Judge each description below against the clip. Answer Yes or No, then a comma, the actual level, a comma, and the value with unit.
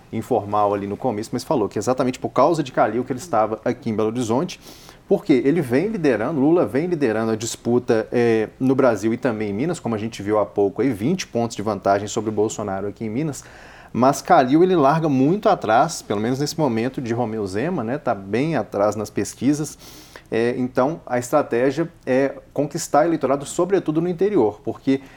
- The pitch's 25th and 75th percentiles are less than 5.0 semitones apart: Yes, average, 4.1 semitones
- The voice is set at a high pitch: No, low, 120 Hz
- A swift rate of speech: Yes, fast, 200 wpm